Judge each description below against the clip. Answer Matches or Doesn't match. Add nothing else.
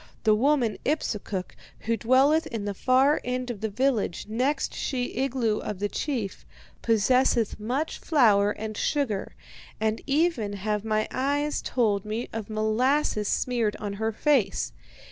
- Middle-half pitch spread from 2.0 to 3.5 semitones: Doesn't match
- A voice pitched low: Doesn't match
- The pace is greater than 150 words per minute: Doesn't match